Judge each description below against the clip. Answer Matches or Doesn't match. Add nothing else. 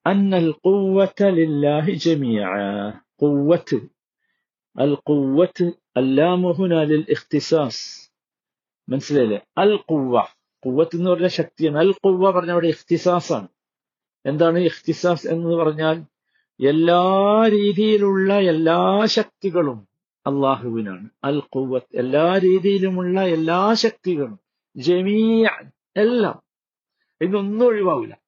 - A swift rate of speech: Doesn't match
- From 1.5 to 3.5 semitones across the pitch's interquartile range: Doesn't match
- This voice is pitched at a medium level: Matches